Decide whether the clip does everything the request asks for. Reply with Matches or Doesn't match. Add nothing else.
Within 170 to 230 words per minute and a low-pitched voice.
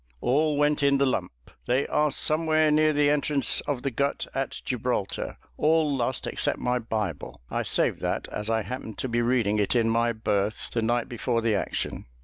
Matches